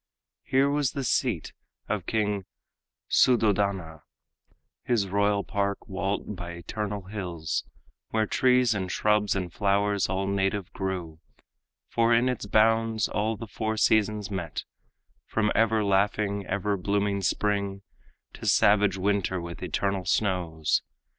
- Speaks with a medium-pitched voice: No, low, 100 Hz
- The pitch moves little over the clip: Yes, narrow, 2.1 semitones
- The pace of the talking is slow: Yes, slow, 125 wpm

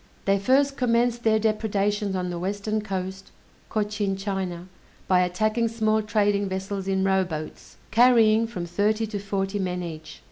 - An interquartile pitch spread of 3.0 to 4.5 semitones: No, narrow, 2.4 semitones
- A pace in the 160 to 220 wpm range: No, average, 145 wpm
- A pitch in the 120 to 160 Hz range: No, high, 200 Hz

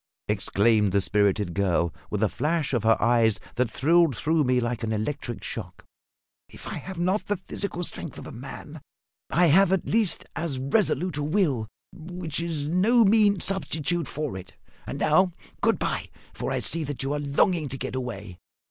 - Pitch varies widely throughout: Yes, wide, 7.2 semitones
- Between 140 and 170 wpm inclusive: No, average, 185 wpm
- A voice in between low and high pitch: Yes, medium, 145 Hz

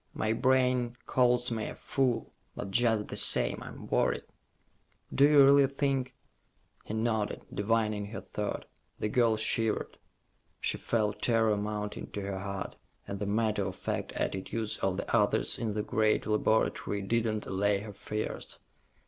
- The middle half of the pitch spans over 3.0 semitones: No, narrow, 2.5 semitones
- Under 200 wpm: Yes, average, 155 wpm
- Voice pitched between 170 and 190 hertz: No, low, 110 Hz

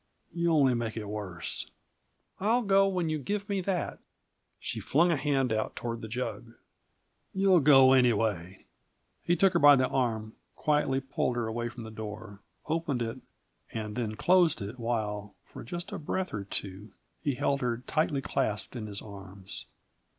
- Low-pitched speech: Yes, low, 125 Hz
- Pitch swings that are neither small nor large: No, wide, 6.2 semitones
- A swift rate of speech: No, average, 170 wpm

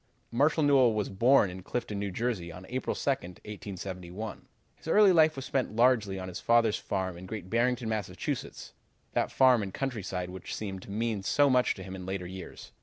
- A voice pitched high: No, low, 105 Hz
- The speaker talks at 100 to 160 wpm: No, average, 190 wpm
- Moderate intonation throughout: Yes, average, 5.0 semitones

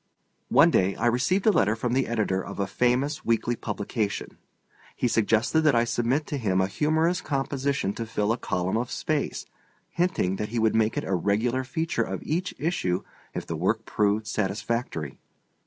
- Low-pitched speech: Yes, low, 115 Hz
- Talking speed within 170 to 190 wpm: Yes, average, 180 wpm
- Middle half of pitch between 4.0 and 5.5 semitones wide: Yes, average, 4.9 semitones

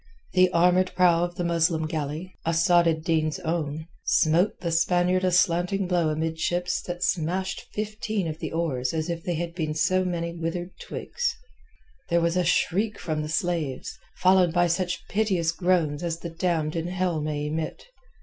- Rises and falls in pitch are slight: Yes, narrow, 2.0 semitones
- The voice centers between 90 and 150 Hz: No, medium, 170 Hz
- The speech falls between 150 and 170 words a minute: Yes, average, 165 wpm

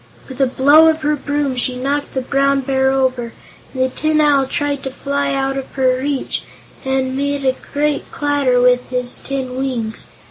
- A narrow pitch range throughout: Yes, narrow, 1.6 semitones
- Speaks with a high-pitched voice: Yes, very high, 270 Hz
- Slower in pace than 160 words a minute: No, average, 185 wpm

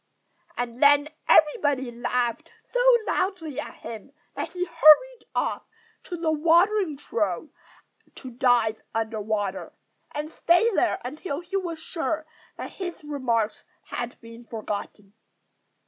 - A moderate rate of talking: No, slow, 125 wpm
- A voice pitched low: No, very high, 290 Hz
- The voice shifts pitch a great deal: Yes, wide, 6.4 semitones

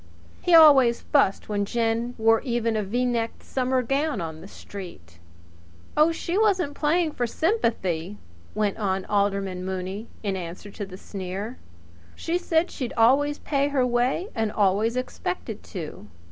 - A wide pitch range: Yes, wide, 6.0 semitones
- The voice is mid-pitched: No, high, 230 Hz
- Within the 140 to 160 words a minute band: Yes, average, 150 wpm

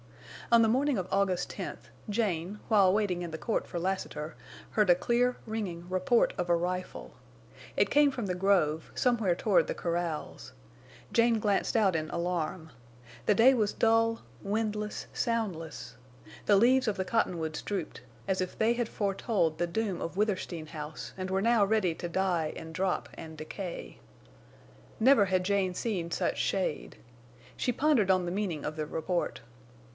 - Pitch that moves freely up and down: No, average, 4.2 semitones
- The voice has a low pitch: No, high, 190 Hz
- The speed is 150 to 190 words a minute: Yes, average, 165 wpm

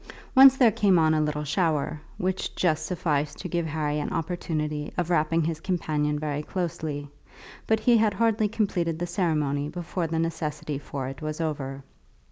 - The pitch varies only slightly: No, average, 3.2 semitones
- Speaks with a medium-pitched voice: Yes, medium, 160 Hz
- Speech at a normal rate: Yes, average, 170 wpm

